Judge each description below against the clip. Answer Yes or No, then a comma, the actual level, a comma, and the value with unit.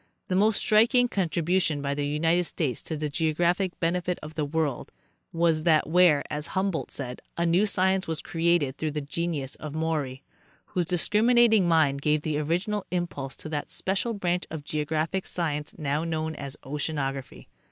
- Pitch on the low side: No, medium, 160 Hz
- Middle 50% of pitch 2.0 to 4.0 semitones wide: Yes, average, 3.3 semitones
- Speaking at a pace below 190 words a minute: Yes, average, 170 wpm